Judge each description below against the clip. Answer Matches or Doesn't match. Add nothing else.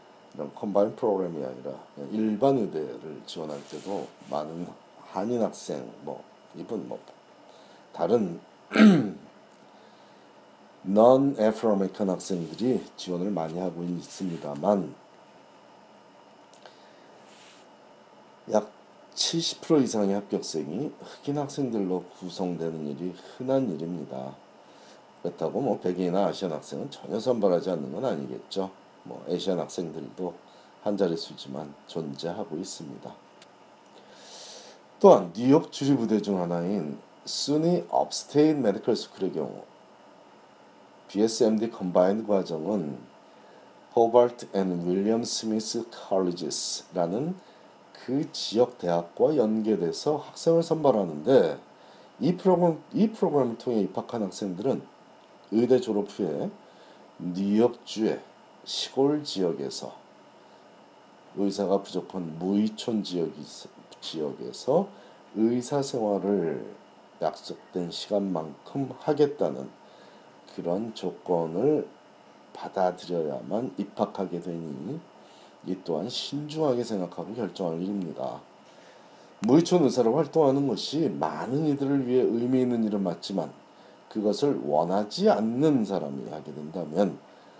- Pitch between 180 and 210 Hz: Doesn't match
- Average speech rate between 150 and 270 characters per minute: Matches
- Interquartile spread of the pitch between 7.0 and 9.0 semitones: Doesn't match